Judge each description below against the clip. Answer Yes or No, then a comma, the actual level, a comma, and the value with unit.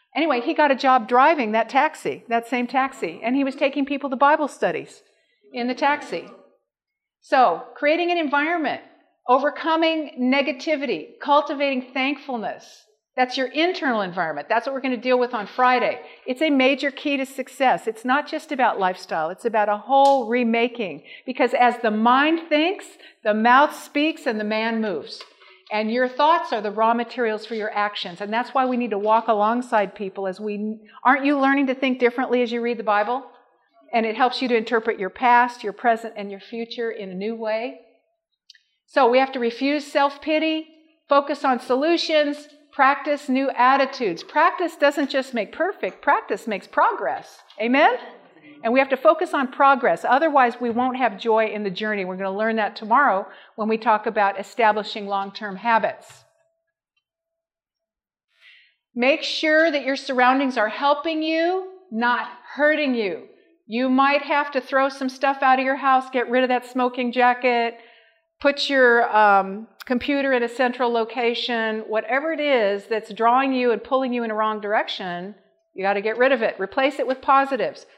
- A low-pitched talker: No, very high, 255 Hz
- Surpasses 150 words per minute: Yes, average, 175 wpm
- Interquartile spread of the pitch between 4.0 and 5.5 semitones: Yes, average, 4.3 semitones